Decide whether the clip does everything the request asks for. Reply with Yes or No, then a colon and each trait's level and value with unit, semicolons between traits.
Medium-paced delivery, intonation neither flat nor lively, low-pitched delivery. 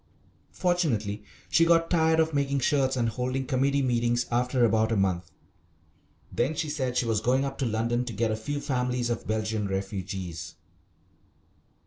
Yes: average, 160 wpm; average, 4.1 semitones; low, 125 Hz